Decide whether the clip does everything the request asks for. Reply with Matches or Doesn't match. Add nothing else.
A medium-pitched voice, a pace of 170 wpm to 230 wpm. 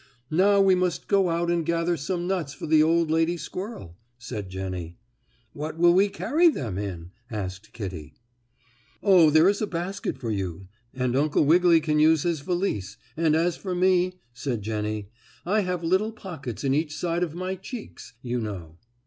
Matches